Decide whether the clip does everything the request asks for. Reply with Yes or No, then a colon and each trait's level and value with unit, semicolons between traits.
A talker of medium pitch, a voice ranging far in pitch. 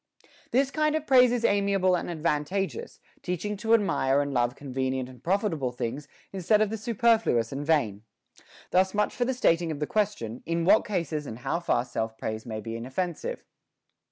Yes: medium, 170 Hz; wide, 8.1 semitones